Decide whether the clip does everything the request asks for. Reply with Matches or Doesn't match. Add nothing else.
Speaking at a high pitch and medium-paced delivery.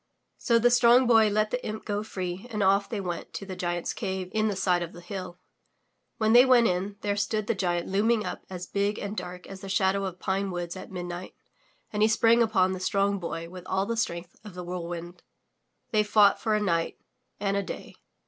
Doesn't match